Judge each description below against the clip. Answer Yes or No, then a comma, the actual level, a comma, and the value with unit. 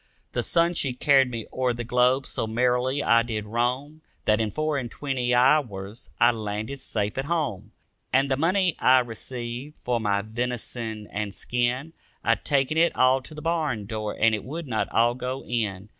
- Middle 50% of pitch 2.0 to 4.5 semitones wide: Yes, average, 3.7 semitones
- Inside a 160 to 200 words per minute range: Yes, average, 185 wpm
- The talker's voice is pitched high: No, low, 125 Hz